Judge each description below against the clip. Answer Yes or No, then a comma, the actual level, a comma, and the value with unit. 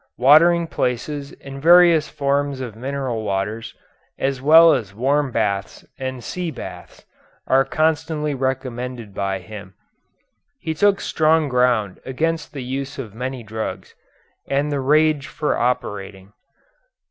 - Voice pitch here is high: No, low, 135 Hz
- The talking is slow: Yes, slow, 125 wpm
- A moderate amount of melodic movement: Yes, average, 4.8 semitones